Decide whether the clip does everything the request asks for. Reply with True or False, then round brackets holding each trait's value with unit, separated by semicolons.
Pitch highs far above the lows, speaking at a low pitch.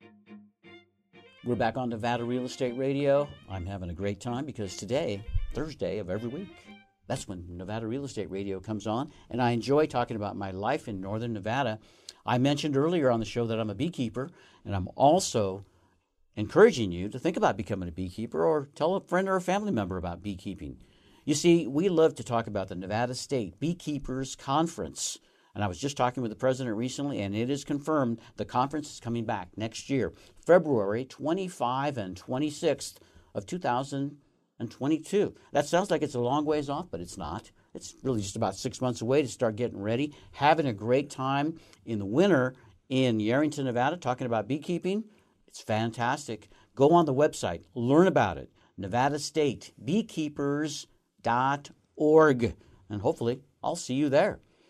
True (5.8 semitones; 125 Hz)